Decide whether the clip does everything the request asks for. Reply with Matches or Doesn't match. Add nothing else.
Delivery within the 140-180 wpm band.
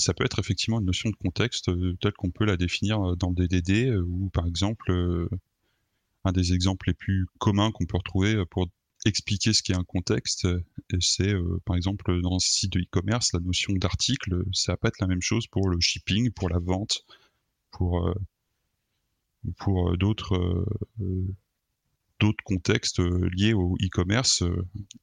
Matches